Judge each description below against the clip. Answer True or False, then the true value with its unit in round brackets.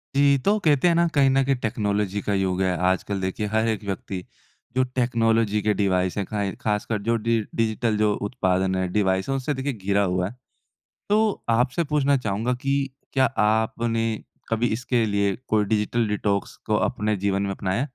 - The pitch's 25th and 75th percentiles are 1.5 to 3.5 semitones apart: False (4.0 semitones)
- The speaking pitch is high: False (110 Hz)